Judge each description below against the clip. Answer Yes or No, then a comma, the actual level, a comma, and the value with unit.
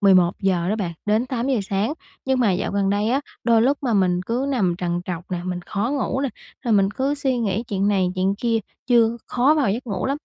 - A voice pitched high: Yes, high, 210 Hz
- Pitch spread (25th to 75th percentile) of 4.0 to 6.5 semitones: Yes, average, 4.7 semitones